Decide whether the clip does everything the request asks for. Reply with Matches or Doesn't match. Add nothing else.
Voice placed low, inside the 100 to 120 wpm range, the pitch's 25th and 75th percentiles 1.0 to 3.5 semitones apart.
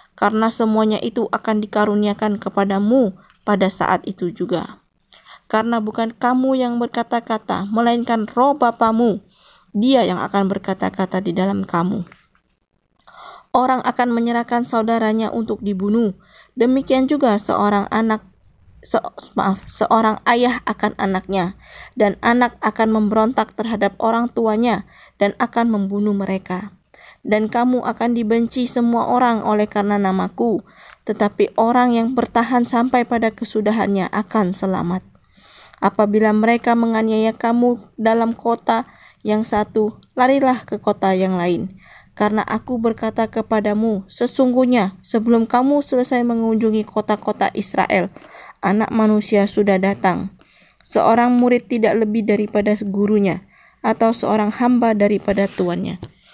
Doesn't match